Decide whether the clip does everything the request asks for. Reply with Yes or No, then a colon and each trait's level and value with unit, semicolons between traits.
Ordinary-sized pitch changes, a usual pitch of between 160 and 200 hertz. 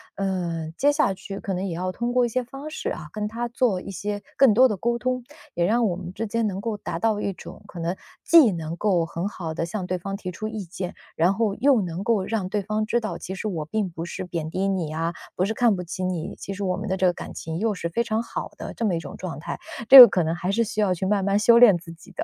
Yes: average, 4.0 semitones; high, 195 Hz